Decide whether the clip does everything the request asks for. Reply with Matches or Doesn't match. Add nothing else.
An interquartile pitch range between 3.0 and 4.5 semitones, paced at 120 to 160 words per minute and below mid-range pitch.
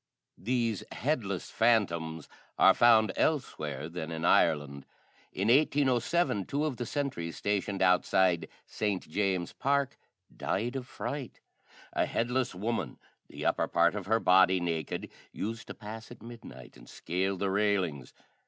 Doesn't match